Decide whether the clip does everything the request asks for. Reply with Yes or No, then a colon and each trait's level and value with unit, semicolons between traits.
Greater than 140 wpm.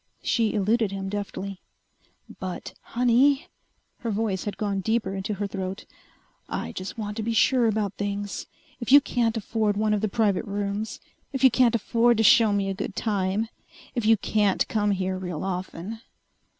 Yes: average, 175 wpm